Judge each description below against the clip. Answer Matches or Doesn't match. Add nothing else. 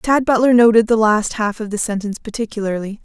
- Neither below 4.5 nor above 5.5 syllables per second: Doesn't match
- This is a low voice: Doesn't match